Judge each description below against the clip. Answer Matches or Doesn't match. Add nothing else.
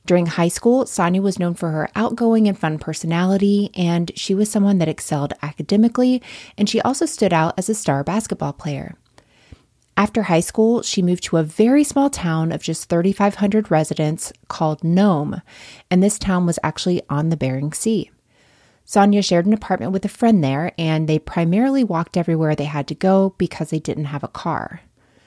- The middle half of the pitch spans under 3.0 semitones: Doesn't match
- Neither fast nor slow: Matches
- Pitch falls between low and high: Matches